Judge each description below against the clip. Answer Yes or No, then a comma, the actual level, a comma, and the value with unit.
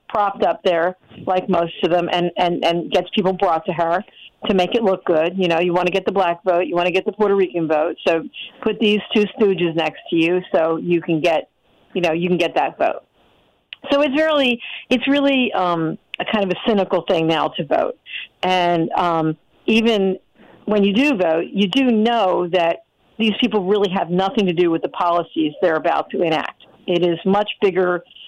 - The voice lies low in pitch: No, medium, 185 Hz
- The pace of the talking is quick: Yes, fast, 210 wpm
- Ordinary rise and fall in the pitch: Yes, average, 3.5 semitones